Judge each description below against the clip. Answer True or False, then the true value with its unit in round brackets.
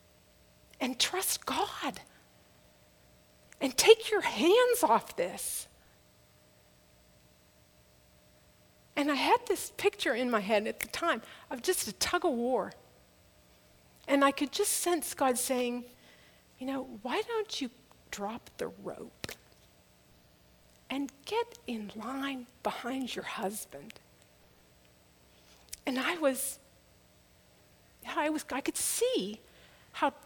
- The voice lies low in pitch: False (245 Hz)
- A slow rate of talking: True (115 wpm)